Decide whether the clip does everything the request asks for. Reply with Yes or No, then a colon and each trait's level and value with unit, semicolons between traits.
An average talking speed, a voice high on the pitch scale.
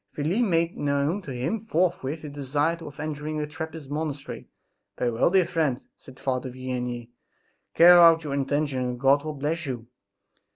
No: average, 165 wpm; medium, 145 Hz